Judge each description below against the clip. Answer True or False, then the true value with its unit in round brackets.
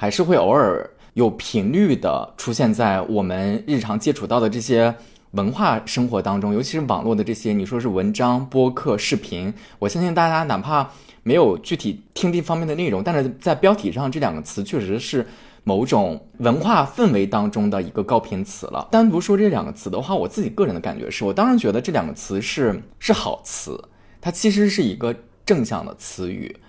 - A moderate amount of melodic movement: False (8.8 semitones)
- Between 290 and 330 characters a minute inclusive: True (300 characters per minute)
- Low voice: True (120 Hz)